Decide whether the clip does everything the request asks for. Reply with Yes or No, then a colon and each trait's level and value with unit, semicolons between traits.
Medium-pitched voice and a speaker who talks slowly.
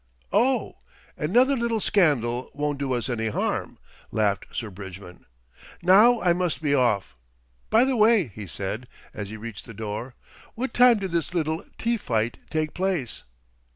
No: medium, 150 Hz; average, 155 wpm